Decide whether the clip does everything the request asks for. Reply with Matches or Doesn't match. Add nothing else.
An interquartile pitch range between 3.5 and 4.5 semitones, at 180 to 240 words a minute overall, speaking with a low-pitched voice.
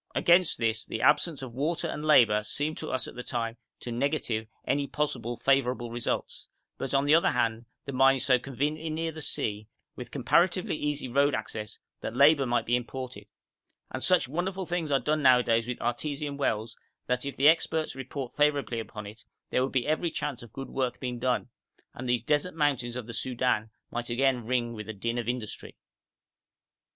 Matches